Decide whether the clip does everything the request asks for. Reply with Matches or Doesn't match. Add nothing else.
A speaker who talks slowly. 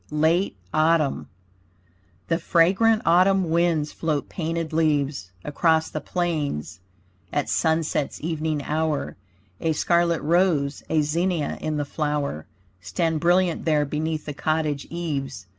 Matches